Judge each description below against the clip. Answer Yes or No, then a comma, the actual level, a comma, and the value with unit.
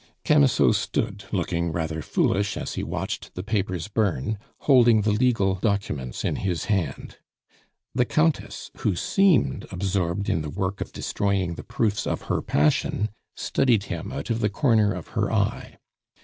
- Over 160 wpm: No, average, 155 wpm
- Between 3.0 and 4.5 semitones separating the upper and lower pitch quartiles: Yes, average, 4.0 semitones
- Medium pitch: No, low, 100 Hz